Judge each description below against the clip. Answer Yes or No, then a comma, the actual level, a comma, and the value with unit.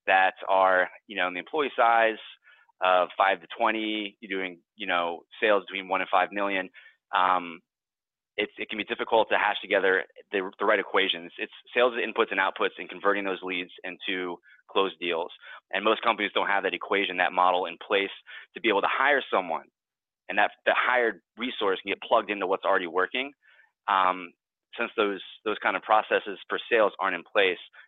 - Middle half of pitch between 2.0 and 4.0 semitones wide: Yes, average, 3.2 semitones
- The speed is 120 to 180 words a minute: No, average, 190 wpm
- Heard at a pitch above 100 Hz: No, very low, 95 Hz